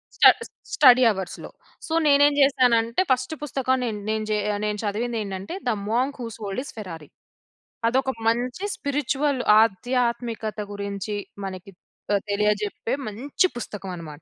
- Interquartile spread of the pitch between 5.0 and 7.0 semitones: No, average, 4.0 semitones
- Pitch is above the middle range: Yes, high, 230 Hz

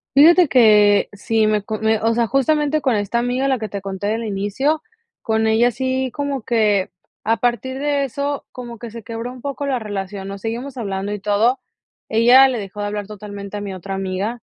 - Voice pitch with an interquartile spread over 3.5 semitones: Yes, average, 4.1 semitones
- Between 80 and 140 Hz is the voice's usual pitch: No, high, 225 Hz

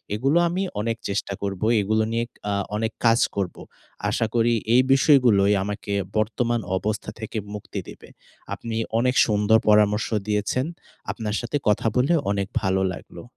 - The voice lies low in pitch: Yes, low, 110 Hz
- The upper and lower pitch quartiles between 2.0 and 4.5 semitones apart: Yes, narrow, 2.5 semitones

